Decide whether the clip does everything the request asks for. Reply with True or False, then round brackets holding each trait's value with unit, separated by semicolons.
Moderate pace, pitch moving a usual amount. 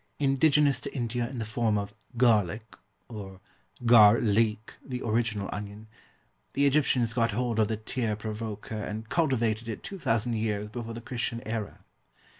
False (150 wpm; 2.2 semitones)